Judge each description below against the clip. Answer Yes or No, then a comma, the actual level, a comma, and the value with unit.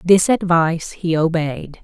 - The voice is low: No, medium, 170 Hz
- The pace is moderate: No, slow, 130 wpm